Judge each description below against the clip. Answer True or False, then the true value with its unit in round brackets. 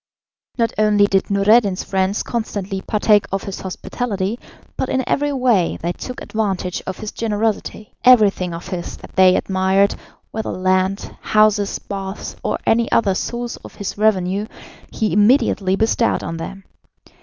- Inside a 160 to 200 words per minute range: False (145 wpm)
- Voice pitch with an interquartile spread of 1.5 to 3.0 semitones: True (2.6 semitones)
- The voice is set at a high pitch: True (205 Hz)